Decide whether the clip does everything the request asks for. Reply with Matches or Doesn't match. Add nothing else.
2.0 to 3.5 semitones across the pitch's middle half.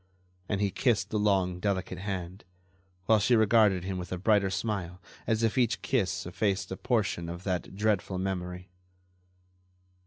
Matches